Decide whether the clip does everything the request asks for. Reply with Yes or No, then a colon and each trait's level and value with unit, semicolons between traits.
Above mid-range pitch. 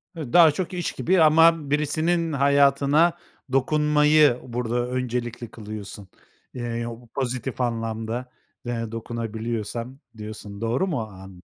No: low, 125 Hz